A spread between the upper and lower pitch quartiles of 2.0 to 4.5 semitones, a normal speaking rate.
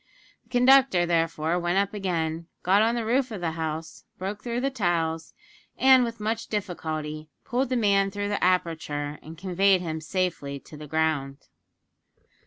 No: average, 5.0 semitones; average, 165 wpm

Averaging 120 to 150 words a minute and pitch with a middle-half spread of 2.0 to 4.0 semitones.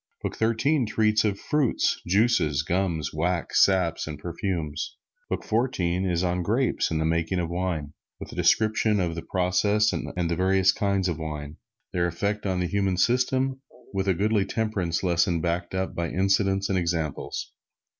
No: average, 165 wpm; average, 3.6 semitones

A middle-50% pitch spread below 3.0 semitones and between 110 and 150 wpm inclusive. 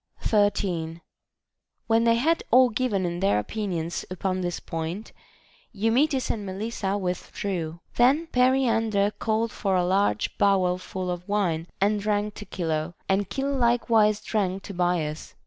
No: average, 4.0 semitones; average, 140 wpm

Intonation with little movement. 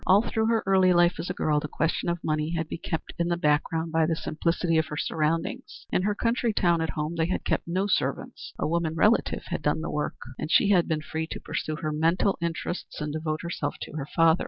Yes: narrow, 2.3 semitones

